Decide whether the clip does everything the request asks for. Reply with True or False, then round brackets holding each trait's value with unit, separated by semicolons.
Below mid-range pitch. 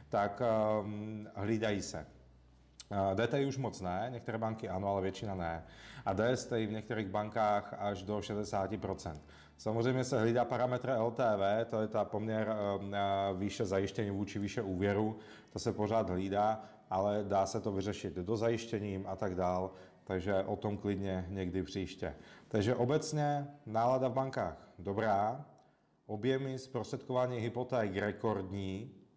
True (105 Hz)